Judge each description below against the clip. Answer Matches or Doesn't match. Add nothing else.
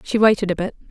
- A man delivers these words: Doesn't match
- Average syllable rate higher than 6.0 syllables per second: Matches